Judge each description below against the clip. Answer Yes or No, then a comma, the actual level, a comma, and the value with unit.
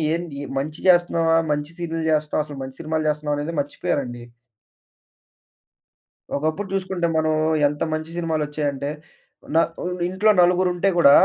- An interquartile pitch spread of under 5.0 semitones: Yes, average, 2.9 semitones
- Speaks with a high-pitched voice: No, medium, 155 Hz